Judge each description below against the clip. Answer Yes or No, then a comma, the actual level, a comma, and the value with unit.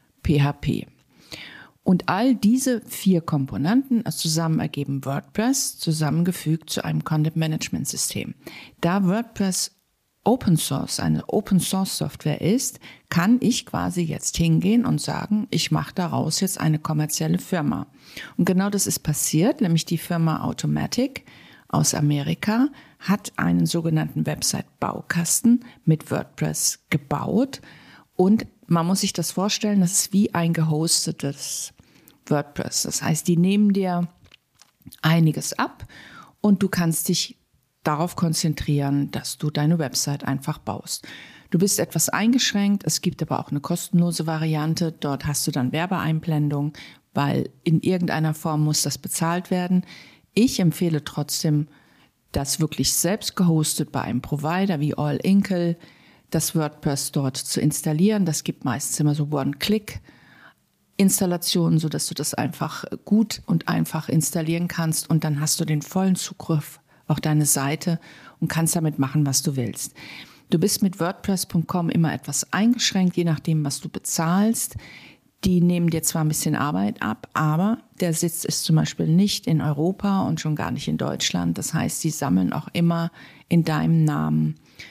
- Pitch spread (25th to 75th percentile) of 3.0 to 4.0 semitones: Yes, average, 3.5 semitones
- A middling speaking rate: Yes, average, 145 wpm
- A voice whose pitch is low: No, medium, 165 Hz